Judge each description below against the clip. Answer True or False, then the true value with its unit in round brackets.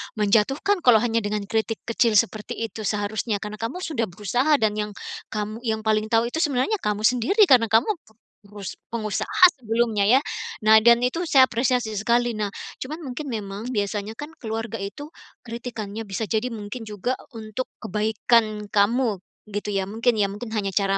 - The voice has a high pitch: True (220 Hz)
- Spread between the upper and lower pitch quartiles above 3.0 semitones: False (2.7 semitones)